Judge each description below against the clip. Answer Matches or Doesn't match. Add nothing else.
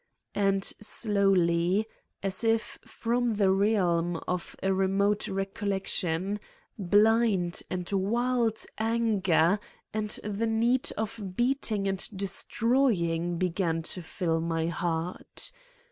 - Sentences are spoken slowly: Matches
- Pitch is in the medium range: Doesn't match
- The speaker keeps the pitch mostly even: Doesn't match